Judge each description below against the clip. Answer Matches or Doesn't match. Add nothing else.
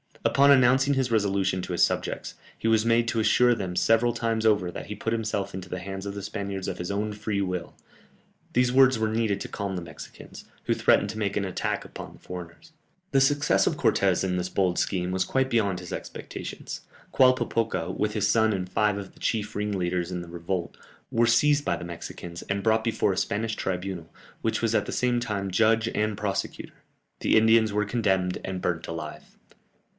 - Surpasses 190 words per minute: Matches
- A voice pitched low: Matches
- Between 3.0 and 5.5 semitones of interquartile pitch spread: Matches